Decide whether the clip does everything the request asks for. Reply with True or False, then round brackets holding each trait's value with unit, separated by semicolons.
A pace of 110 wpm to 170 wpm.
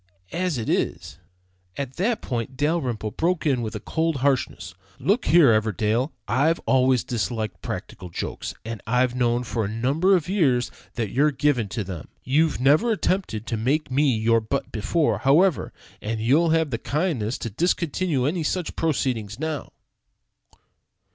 True (155 wpm)